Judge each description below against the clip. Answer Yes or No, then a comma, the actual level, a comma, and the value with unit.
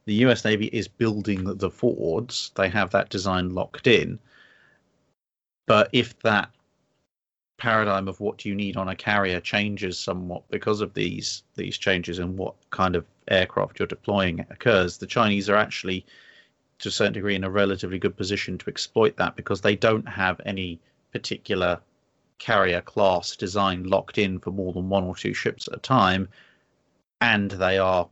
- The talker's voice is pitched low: Yes, very low, 95 Hz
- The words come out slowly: No, average, 170 wpm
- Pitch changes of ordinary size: No, narrow, 2.0 semitones